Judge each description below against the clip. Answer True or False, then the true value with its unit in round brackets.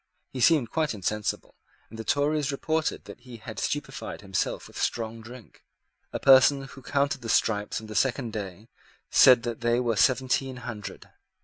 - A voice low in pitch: True (120 Hz)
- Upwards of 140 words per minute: True (170 wpm)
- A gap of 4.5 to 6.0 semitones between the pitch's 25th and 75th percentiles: False (3.6 semitones)